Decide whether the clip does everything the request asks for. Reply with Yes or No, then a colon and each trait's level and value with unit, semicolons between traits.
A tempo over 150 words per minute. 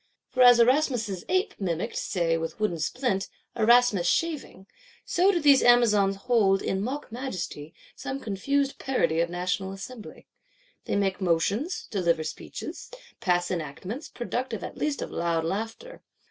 No: average, 140 wpm